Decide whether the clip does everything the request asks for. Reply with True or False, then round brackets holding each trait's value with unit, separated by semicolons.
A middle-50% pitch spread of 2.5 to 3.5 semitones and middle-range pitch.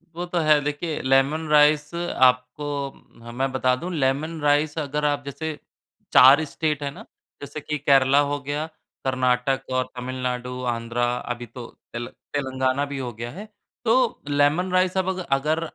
True (3.1 semitones; 145 Hz)